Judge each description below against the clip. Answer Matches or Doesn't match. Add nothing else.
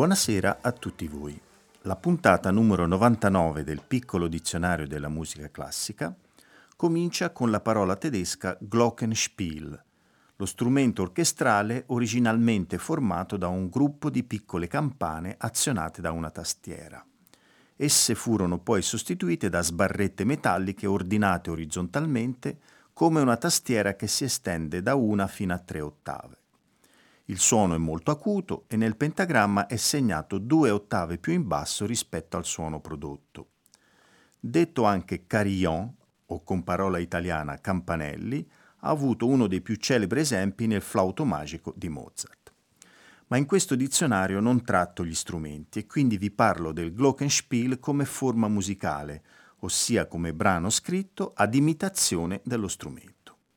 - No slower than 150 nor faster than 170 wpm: Doesn't match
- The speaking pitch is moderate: Doesn't match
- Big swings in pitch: Matches